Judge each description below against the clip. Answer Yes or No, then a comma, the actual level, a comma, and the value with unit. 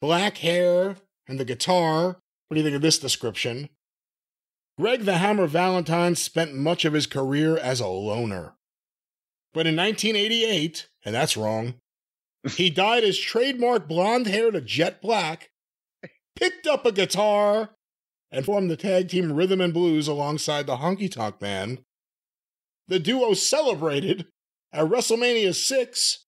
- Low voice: No, medium, 175 Hz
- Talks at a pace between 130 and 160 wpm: Yes, average, 145 wpm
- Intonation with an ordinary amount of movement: No, wide, 5.7 semitones